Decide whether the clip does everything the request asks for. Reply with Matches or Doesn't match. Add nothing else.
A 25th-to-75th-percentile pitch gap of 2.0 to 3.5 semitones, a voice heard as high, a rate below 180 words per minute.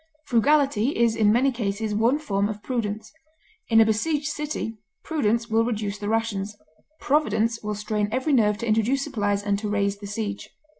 Matches